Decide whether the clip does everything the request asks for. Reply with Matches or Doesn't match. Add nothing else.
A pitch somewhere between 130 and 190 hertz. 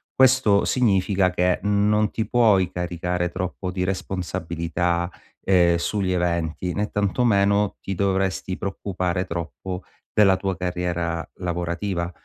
Doesn't match